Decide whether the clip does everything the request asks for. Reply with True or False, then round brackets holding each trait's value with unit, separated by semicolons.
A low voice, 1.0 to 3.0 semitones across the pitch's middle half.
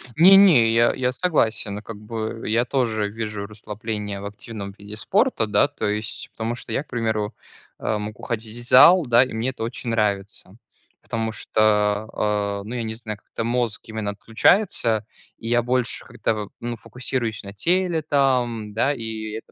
True (110 Hz; 2.6 semitones)